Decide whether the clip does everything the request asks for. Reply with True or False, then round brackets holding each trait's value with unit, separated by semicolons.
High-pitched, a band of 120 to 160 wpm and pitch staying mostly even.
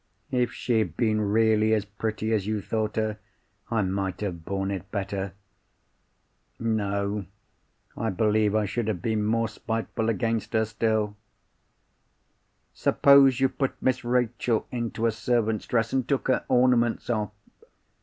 False (110 Hz; 145 wpm; 2.1 semitones)